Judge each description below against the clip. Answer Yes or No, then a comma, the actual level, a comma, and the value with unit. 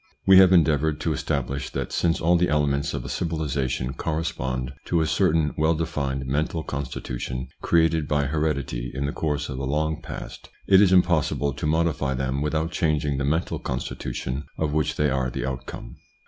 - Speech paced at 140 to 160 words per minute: No, average, 180 wpm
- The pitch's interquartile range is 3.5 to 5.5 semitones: No, average, 3.1 semitones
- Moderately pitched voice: No, very low, 75 Hz